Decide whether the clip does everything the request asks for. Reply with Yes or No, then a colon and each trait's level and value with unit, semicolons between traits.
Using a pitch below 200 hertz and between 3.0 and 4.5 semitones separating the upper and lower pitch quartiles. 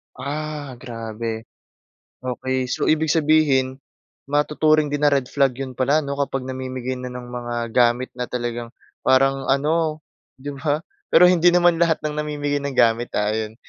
Yes: low, 135 Hz; average, 3.3 semitones